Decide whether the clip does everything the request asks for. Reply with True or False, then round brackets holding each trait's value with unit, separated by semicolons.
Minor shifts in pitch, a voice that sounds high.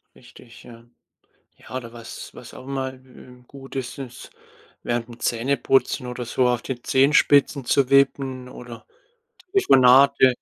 False (1.9 semitones; 130 Hz)